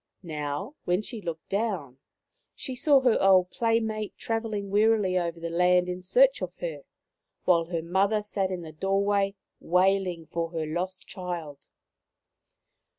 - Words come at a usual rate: Yes, average, 150 wpm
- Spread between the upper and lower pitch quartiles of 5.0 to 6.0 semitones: No, average, 3.6 semitones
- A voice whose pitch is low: No, medium, 185 Hz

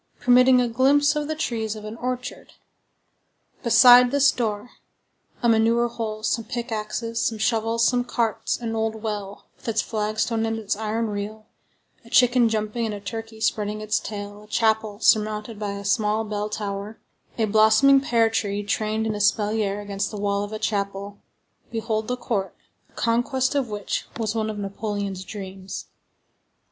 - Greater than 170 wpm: No, average, 160 wpm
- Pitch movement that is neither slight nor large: No, narrow, 1.9 semitones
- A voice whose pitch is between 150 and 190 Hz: No, high, 220 Hz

